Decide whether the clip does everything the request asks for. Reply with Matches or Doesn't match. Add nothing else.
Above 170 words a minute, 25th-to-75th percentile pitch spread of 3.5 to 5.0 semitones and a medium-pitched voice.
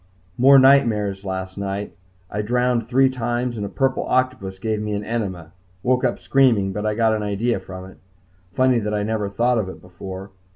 Doesn't match